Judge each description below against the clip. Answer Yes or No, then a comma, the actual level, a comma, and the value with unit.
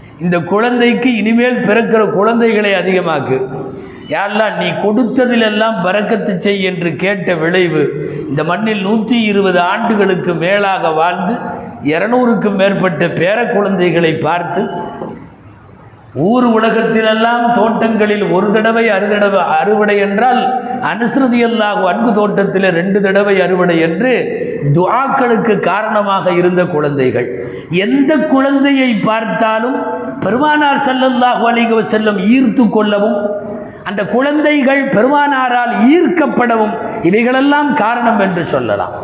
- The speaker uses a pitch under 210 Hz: No, high, 215 Hz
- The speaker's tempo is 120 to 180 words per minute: No, average, 95 wpm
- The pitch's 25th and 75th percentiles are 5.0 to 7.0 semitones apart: No, average, 4.3 semitones